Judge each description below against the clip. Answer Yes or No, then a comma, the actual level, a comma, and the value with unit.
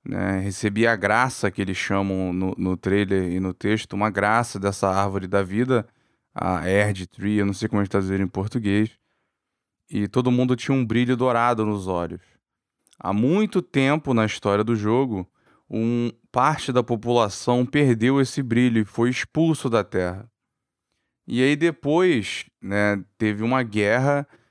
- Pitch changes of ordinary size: Yes, average, 4.1 semitones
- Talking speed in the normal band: Yes, average, 160 wpm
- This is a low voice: Yes, low, 110 Hz